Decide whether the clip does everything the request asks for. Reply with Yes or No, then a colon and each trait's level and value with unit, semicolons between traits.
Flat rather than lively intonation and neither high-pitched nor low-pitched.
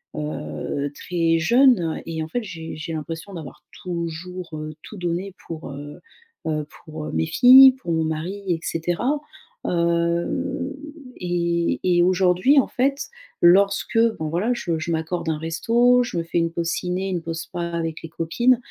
No: average, 3.0 semitones; medium, 170 Hz